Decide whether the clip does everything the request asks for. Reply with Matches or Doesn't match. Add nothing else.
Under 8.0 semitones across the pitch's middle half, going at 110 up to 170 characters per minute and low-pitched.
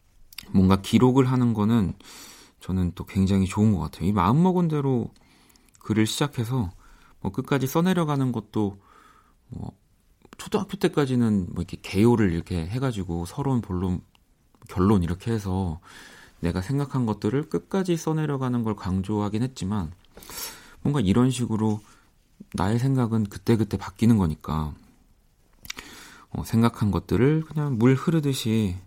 Doesn't match